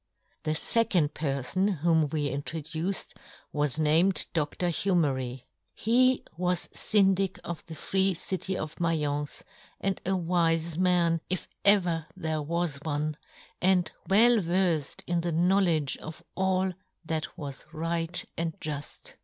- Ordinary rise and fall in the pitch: Yes, average, 3.3 semitones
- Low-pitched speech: No, medium, 165 Hz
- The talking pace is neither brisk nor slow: No, slow, 130 wpm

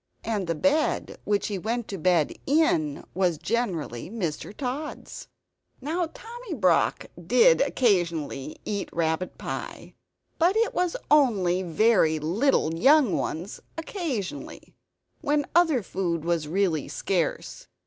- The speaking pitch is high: Yes, high, 205 Hz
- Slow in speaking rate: Yes, slow, 120 wpm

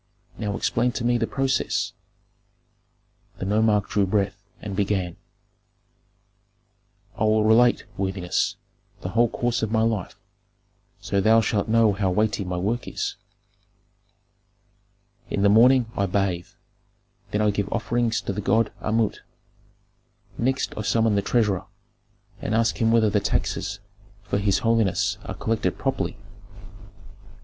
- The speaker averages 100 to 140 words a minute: Yes, slow, 135 wpm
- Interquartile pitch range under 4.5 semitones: Yes, narrow, 2.4 semitones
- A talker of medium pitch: No, low, 105 Hz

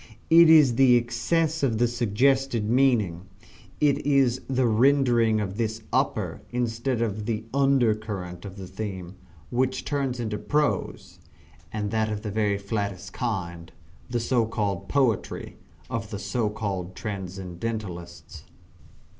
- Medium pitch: No, low, 110 Hz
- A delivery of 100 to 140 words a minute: Yes, slow, 135 wpm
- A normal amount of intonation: Yes, average, 4.2 semitones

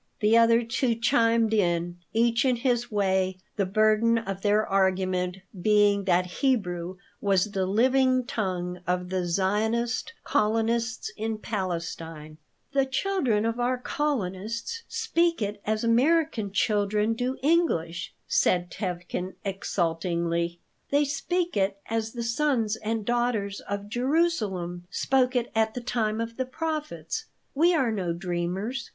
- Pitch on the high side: Yes, high, 215 Hz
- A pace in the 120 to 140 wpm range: Yes, slow, 135 wpm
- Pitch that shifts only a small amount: No, average, 4.6 semitones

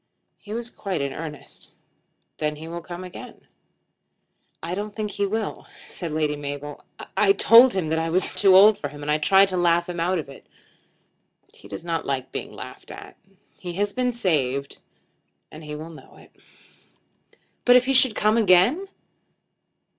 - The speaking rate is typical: Yes, average, 175 wpm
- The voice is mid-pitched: Yes, medium, 175 Hz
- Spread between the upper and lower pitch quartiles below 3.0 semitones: No, average, 5.2 semitones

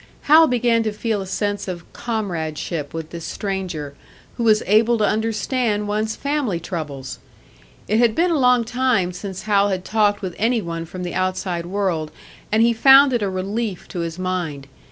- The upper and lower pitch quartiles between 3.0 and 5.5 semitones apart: Yes, average, 4.5 semitones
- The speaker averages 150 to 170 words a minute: No, average, 180 wpm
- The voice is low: No, high, 205 Hz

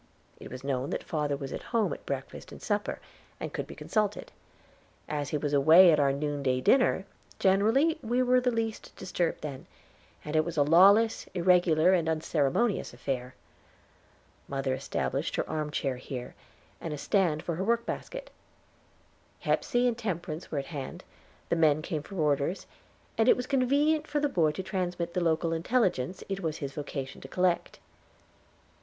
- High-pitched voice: No, medium, 170 Hz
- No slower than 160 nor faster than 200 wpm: Yes, average, 170 wpm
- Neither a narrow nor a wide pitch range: No, wide, 6.2 semitones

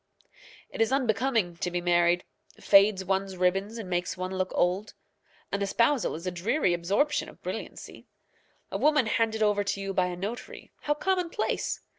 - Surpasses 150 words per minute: Yes, average, 165 wpm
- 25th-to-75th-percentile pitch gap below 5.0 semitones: Yes, average, 4.0 semitones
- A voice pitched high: Yes, high, 195 Hz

